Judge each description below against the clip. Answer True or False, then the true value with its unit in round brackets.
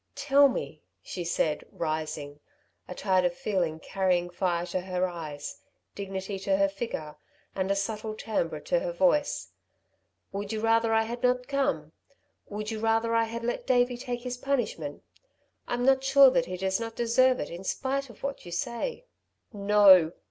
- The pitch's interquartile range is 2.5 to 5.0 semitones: False (5.4 semitones)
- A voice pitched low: False (205 Hz)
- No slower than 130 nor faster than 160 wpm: False (170 wpm)